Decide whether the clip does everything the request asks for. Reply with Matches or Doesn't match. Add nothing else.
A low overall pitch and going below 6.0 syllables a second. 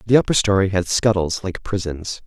Matches